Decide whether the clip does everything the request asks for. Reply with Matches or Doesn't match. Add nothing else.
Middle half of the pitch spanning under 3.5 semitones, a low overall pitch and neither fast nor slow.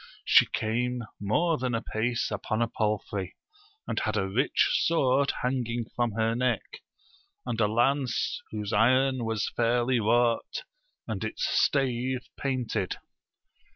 Doesn't match